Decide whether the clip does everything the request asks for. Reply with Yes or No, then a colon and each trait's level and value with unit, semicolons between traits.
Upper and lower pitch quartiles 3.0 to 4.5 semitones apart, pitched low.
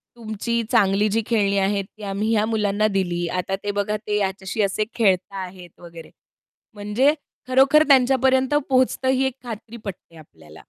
No: average, 3.6 semitones; high, 210 Hz